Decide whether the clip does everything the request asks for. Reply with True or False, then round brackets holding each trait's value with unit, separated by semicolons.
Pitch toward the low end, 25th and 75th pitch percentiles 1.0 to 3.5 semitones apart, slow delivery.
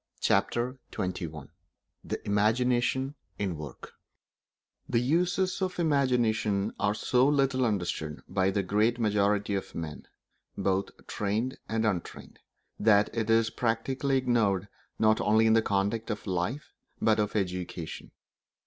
False (110 Hz; 3.9 semitones; 130 wpm)